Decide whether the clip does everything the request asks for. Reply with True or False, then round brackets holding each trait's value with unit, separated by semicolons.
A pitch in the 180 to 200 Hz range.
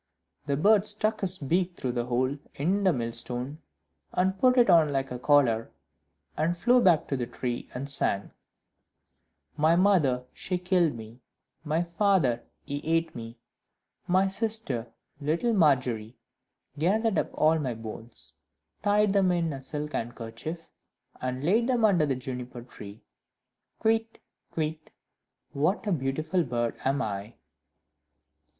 False (150 Hz)